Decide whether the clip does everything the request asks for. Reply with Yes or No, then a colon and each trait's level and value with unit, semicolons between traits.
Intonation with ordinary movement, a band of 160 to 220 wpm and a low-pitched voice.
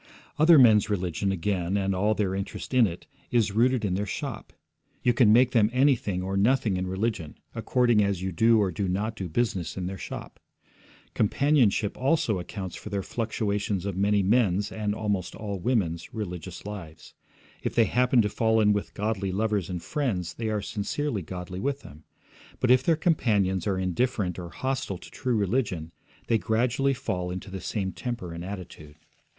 Yes: average, 3.9 semitones; average, 180 wpm; low, 105 Hz